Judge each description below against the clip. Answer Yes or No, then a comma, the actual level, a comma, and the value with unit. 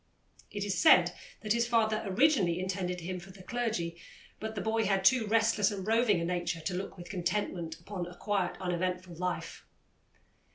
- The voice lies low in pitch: No, high, 190 Hz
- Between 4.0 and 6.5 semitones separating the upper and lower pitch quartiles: No, average, 3.4 semitones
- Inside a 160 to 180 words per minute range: Yes, average, 175 wpm